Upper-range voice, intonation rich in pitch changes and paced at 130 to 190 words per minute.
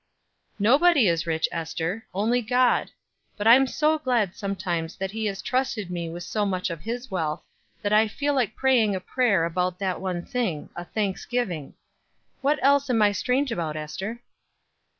Yes: high, 205 Hz; wide, 6.0 semitones; average, 170 wpm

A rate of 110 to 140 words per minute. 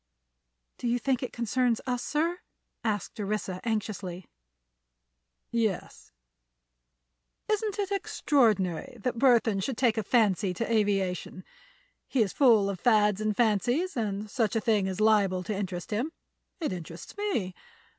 Yes: slow, 135 wpm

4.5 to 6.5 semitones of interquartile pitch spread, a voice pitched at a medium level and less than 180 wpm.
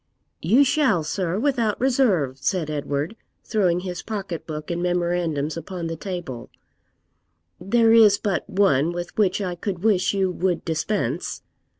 No: average, 3.9 semitones; medium, 180 Hz; average, 140 wpm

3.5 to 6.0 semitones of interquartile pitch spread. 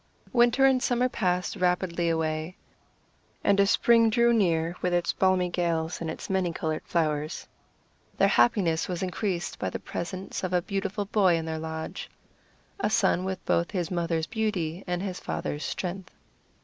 No: average, 3.0 semitones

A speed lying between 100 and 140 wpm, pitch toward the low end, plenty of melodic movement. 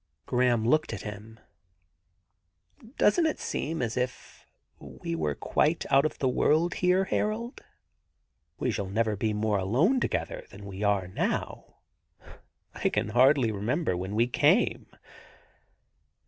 Yes: slow, 135 wpm; low, 120 Hz; wide, 7.0 semitones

